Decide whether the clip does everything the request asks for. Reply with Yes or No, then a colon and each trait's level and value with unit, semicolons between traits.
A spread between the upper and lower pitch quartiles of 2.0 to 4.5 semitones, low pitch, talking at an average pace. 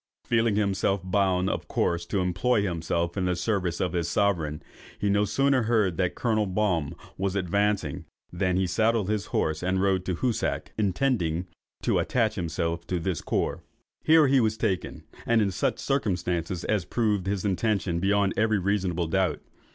Yes: average, 3.3 semitones; very low, 95 Hz; average, 165 wpm